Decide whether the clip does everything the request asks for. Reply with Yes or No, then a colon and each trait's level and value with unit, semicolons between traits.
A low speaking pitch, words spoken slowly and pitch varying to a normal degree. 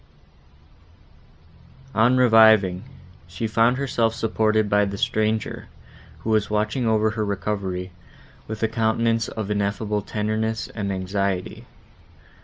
No: low, 110 Hz; slow, 110 wpm; narrow, 1.8 semitones